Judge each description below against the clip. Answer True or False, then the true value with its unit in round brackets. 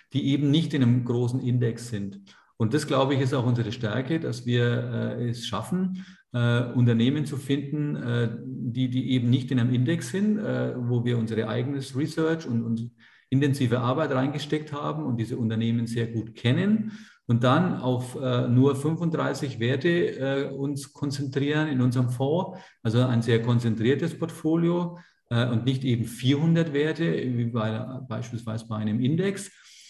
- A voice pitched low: True (130 Hz)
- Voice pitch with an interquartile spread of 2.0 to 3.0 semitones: False (3.7 semitones)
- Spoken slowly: False (165 wpm)